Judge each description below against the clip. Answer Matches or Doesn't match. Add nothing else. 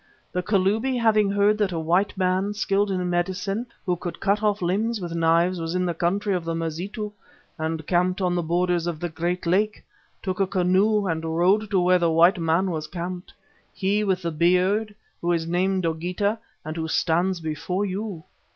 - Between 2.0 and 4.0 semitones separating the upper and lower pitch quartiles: Matches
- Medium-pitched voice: Matches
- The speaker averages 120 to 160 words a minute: Doesn't match